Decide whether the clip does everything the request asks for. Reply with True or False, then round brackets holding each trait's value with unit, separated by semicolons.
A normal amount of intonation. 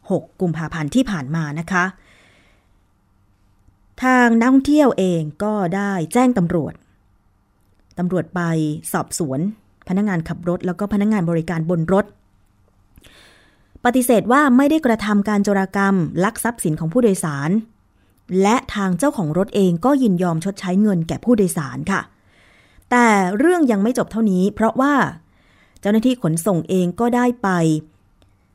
False (5.8 semitones)